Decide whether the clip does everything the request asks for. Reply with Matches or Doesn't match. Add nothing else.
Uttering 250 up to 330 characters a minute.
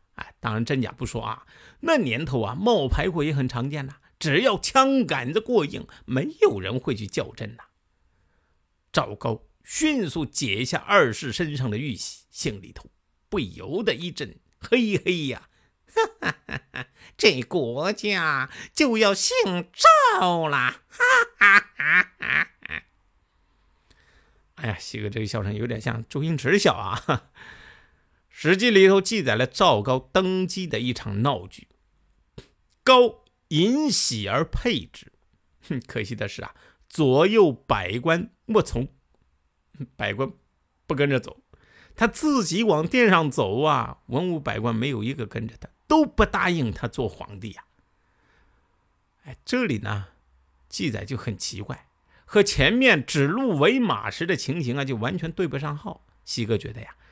Doesn't match